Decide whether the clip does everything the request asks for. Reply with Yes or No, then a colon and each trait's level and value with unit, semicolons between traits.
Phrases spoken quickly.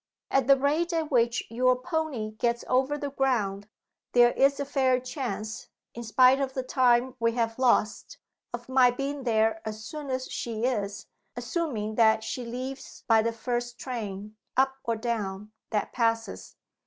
No: average, 165 wpm